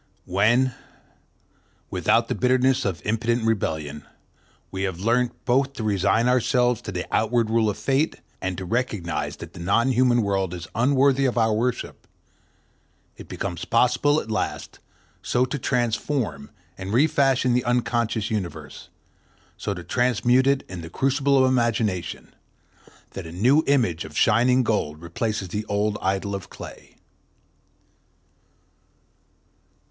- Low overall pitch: Yes, low, 115 Hz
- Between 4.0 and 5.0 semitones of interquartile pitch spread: Yes, average, 4.6 semitones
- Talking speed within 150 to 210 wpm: No, slow, 135 wpm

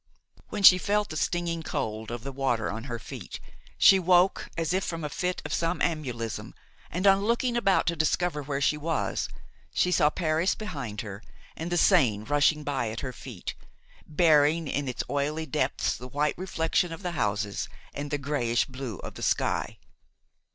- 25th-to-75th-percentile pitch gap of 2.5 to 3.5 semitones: No, wide, 5.4 semitones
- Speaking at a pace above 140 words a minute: Yes, average, 175 wpm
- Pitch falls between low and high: Yes, medium, 150 Hz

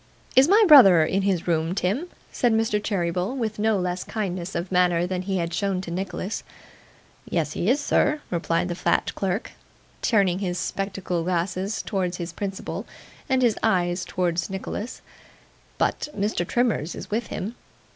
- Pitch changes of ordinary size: Yes, average, 3.2 semitones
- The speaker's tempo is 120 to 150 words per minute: No, average, 160 wpm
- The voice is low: No, high, 190 Hz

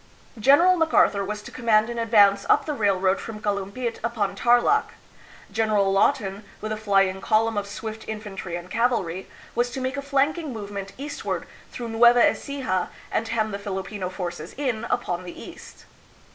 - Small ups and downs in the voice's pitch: No, average, 3.4 semitones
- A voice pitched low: No, high, 215 Hz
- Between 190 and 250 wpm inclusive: No, average, 160 wpm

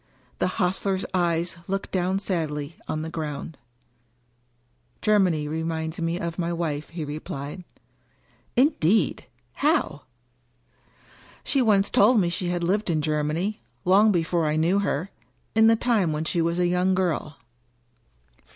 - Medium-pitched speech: Yes, medium, 175 Hz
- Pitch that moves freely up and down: No, average, 3.6 semitones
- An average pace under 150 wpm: Yes, average, 140 wpm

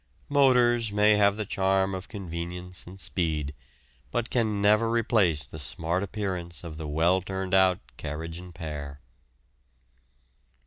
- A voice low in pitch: Yes, very low, 95 Hz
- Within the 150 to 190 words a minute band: No, slow, 135 wpm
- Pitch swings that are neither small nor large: Yes, average, 4.0 semitones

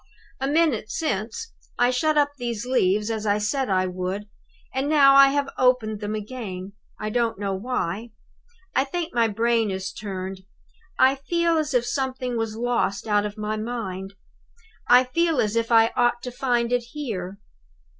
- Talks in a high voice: Yes, high, 235 Hz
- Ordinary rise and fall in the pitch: Yes, average, 4.1 semitones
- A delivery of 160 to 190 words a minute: Yes, average, 170 wpm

